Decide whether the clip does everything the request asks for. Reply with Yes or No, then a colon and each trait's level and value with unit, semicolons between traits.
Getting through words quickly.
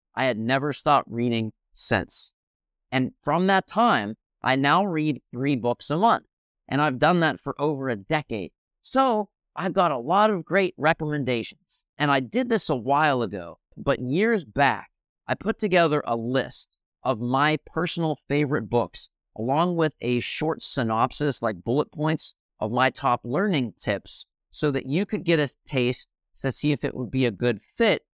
No: average, 175 wpm